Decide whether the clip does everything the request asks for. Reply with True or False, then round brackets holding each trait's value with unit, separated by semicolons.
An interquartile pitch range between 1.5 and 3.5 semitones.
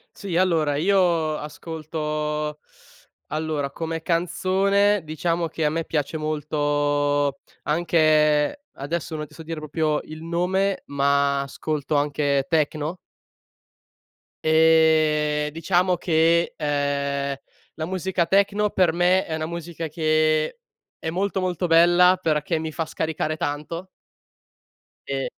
True (2.4 semitones)